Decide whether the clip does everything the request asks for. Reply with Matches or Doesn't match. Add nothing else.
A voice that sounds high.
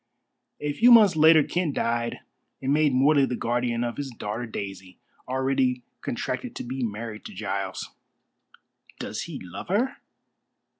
Doesn't match